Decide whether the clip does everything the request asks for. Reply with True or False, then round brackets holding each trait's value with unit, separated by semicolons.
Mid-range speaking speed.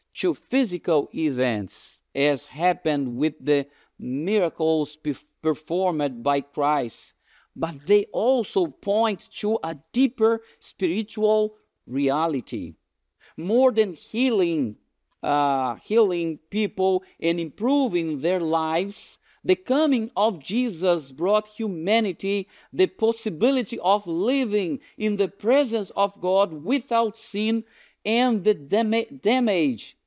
False (100 wpm)